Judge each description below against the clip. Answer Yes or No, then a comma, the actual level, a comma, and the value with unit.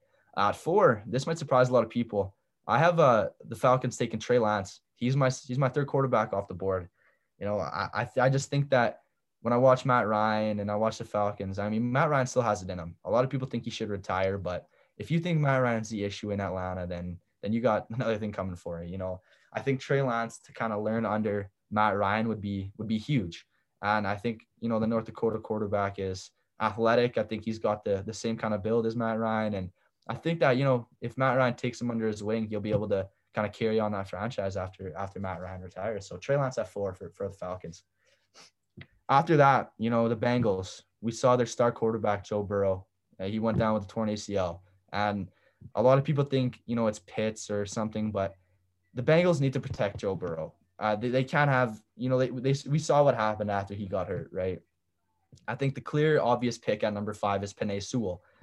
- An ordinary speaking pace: No, fast, 240 wpm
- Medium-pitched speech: No, low, 110 Hz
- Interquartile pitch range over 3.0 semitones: Yes, average, 3.8 semitones